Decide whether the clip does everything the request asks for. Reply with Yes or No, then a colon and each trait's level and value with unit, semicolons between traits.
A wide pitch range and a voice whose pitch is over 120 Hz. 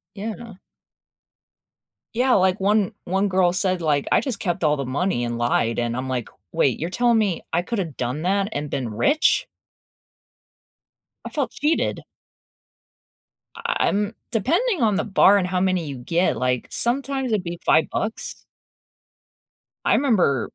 Yes: wide, 7.3 semitones; medium, 185 Hz